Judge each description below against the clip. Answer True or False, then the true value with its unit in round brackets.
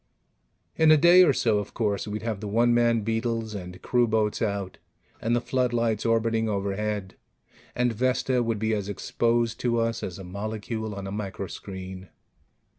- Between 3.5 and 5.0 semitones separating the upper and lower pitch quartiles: False (2.7 semitones)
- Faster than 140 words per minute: True (165 wpm)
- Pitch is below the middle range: True (110 Hz)